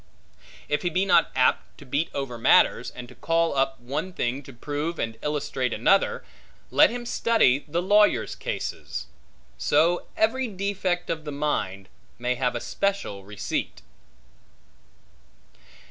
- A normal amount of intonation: No, wide, 6.6 semitones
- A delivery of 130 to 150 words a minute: Yes, average, 140 wpm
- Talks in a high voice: No, medium, 150 Hz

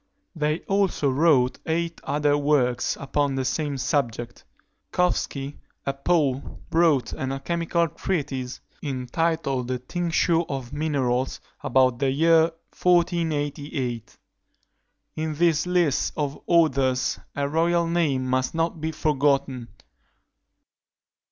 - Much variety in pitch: No, average, 3.8 semitones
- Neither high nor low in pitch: Yes, medium, 145 Hz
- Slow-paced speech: Yes, slow, 105 wpm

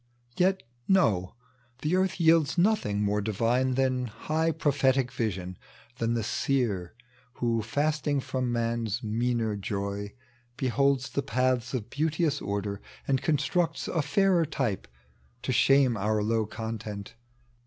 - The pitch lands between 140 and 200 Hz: No, low, 125 Hz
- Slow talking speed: Yes, slow, 130 wpm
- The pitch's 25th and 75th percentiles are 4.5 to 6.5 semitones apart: Yes, average, 5.1 semitones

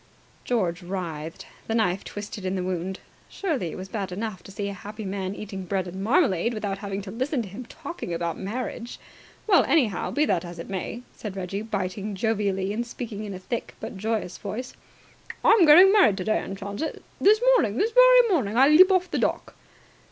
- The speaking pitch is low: No, high, 205 Hz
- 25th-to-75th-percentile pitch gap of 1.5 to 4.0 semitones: No, average, 4.7 semitones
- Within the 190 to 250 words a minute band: Yes, average, 200 wpm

